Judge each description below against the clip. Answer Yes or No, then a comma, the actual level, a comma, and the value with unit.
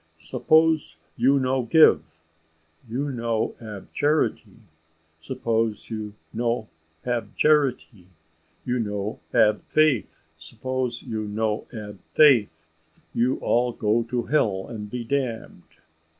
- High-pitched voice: No, low, 115 Hz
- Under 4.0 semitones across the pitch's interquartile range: Yes, average, 3.5 semitones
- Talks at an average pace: No, slow, 110 wpm